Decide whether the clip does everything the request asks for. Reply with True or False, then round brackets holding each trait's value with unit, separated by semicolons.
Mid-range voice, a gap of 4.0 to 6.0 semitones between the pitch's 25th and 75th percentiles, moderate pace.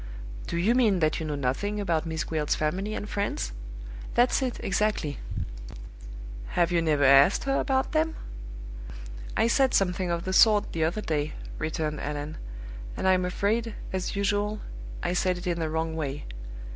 True (180 Hz; 5.0 semitones; 165 wpm)